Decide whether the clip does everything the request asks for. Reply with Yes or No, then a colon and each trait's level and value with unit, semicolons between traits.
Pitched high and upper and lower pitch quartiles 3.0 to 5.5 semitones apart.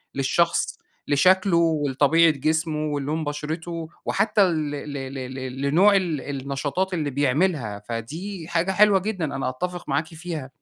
No: medium, 155 Hz; average, 4.0 semitones